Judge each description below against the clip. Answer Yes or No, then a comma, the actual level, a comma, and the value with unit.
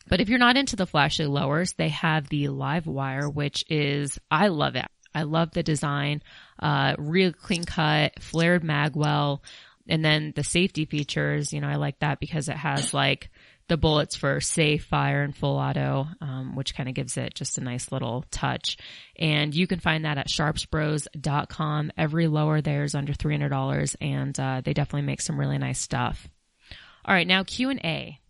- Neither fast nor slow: Yes, average, 195 wpm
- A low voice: No, medium, 150 Hz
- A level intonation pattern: Yes, narrow, 1.9 semitones